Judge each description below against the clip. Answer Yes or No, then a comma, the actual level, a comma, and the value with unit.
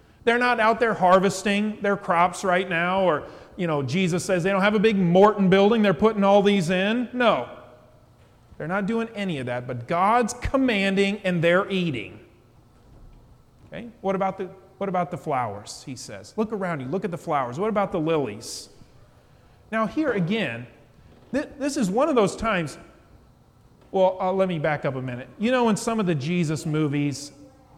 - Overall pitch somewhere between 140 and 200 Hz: Yes, medium, 185 Hz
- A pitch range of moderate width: No, wide, 6.5 semitones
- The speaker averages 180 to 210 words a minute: Yes, average, 185 wpm